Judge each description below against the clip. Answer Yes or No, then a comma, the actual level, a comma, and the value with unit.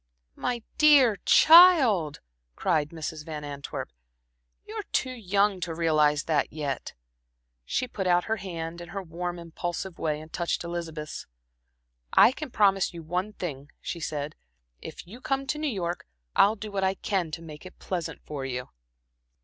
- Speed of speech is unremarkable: Yes, average, 160 wpm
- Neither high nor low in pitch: Yes, medium, 175 Hz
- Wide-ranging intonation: No, average, 4.8 semitones